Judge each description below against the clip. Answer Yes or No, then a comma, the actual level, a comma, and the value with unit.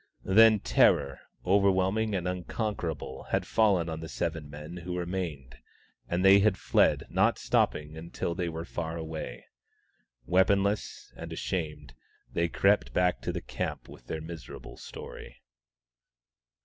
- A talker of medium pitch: No, very low, 85 Hz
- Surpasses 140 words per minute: No, slow, 135 wpm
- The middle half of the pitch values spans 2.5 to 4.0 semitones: Yes, average, 3.4 semitones